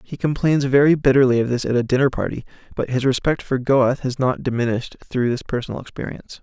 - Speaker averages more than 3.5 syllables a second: Yes, 6.5 syllables/s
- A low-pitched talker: Yes, low, 130 Hz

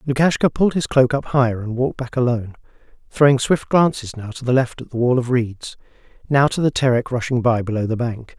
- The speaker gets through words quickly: Yes, fast, 220 wpm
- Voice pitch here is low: Yes, low, 125 Hz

